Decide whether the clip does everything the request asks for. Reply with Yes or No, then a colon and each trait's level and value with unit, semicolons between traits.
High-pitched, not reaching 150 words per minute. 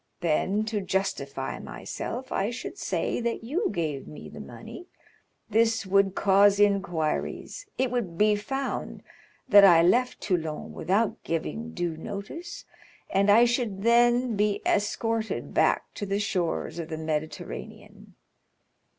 Yes: high, 205 Hz; slow, 135 wpm